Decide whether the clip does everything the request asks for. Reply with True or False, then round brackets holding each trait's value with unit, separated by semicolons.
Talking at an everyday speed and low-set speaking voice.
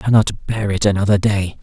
False (220 wpm; 100 Hz)